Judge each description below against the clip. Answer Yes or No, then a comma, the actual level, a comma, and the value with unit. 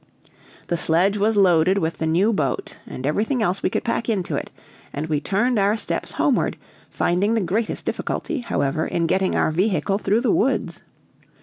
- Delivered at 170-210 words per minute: Yes, average, 180 wpm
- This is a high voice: Yes, high, 195 Hz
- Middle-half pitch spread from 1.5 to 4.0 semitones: No, average, 4.7 semitones